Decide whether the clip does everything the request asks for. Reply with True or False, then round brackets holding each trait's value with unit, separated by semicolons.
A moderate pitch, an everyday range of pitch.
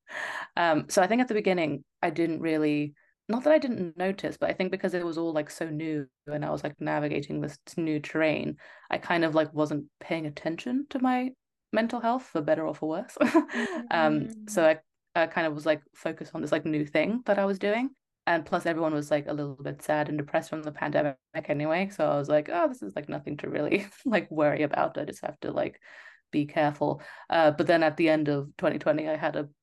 True (160 Hz; 4.0 semitones)